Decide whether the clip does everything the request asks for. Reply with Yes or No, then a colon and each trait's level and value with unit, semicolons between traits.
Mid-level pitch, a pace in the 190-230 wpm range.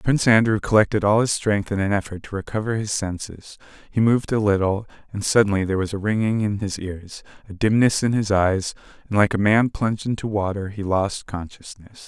No: low, 105 Hz; fast, 205 wpm